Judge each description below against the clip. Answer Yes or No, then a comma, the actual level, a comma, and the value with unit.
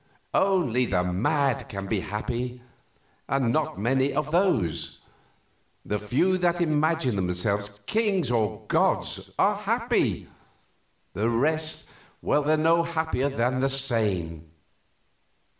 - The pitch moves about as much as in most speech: No, wide, 7.0 semitones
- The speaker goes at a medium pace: No, slow, 110 wpm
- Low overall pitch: Yes, low, 130 Hz